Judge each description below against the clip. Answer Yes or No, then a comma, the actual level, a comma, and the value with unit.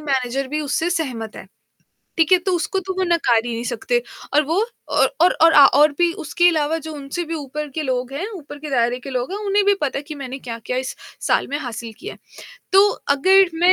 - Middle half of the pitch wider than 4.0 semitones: Yes, average, 5.1 semitones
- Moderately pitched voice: No, very high, 295 Hz